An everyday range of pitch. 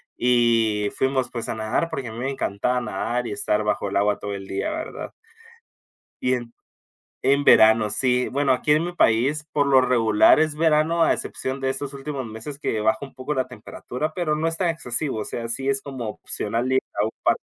Yes: average, 4.3 semitones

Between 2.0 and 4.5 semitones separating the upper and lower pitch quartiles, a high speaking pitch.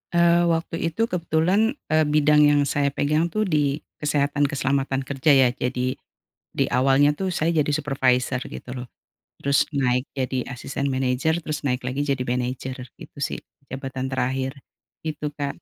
No: average, 2.9 semitones; medium, 140 Hz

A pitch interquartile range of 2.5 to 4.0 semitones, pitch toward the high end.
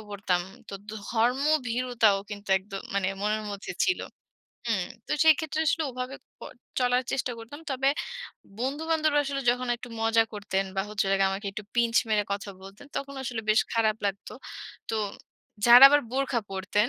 No: average, 4.4 semitones; high, 230 Hz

